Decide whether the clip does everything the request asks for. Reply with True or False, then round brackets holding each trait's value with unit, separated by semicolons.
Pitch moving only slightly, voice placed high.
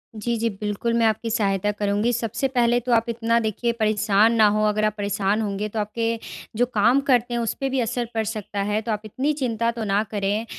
True (2.1 semitones; 220 Hz)